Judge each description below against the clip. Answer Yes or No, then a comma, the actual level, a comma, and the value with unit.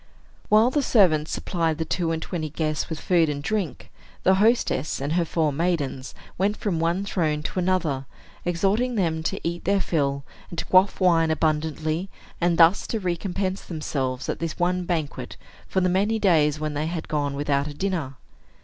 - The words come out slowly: No, average, 180 wpm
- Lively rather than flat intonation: No, average, 3.4 semitones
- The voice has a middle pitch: Yes, medium, 165 Hz